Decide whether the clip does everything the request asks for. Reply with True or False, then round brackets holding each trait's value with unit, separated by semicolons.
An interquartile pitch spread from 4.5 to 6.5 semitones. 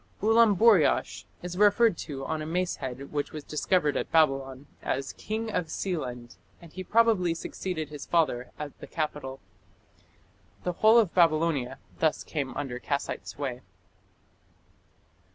True (5.0 semitones)